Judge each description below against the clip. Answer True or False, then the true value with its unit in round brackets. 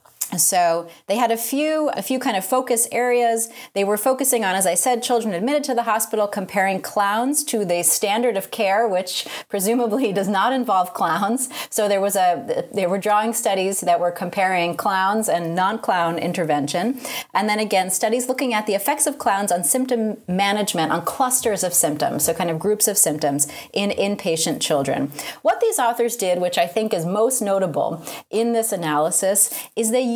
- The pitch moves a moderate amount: True (4.8 semitones)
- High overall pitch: True (205 Hz)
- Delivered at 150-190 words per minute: True (185 wpm)